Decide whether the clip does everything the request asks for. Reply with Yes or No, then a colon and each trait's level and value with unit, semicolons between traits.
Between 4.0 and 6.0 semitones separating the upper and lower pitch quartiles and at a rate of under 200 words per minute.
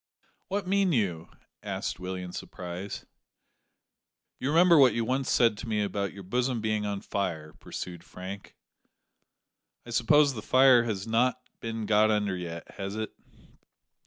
Yes: average, 4.6 semitones; average, 150 wpm